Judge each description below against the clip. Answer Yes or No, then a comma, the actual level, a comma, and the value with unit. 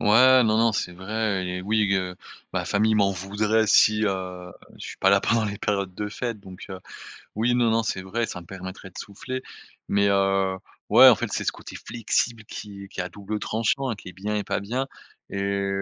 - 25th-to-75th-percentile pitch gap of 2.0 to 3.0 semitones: Yes, narrow, 2.5 semitones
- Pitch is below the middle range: Yes, low, 100 Hz